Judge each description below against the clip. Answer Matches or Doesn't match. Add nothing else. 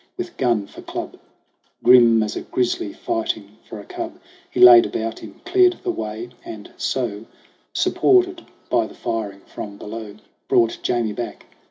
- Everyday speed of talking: Matches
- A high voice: Doesn't match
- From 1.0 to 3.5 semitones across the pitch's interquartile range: Matches